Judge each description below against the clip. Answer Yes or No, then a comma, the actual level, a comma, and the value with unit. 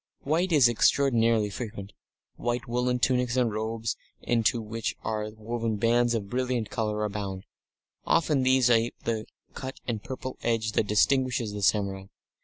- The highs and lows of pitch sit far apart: No, average, 2.7 semitones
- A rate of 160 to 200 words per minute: No, average, 145 wpm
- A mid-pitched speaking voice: No, low, 115 Hz